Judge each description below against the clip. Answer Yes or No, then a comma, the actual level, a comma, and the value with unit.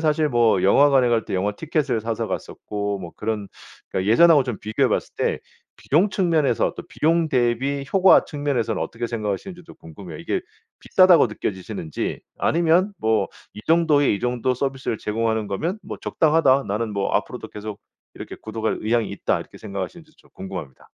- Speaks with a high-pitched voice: No, low, 120 Hz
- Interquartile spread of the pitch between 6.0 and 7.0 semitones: Yes, wide, 6.5 semitones